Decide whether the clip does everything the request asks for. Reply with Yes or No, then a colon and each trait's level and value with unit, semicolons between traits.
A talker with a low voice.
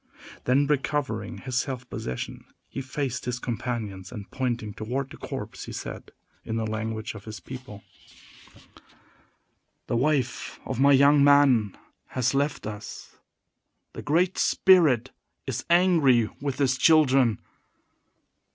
Yes: low, 130 Hz